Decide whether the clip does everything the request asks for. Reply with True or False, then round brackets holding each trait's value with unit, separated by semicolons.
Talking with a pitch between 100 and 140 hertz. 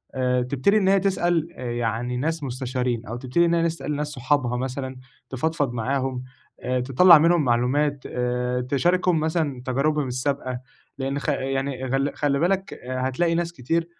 True (135 Hz)